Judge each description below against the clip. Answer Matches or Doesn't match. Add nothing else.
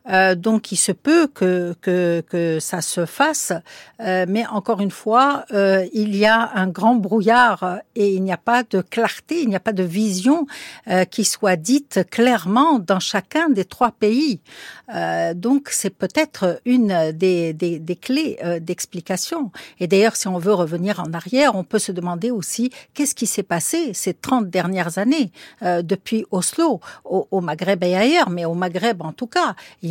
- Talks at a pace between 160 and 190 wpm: Matches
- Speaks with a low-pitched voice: Doesn't match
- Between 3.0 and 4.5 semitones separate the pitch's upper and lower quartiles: Doesn't match